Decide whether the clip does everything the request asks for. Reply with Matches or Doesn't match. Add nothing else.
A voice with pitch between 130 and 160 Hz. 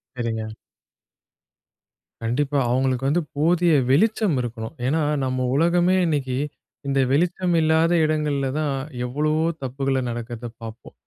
Matches